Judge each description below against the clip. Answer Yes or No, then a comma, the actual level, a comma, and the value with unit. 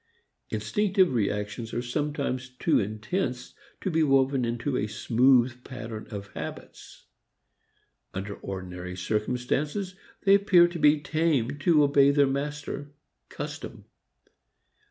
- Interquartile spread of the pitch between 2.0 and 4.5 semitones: No, average, 5.0 semitones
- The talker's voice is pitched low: Yes, low, 130 Hz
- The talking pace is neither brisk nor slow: No, slow, 115 wpm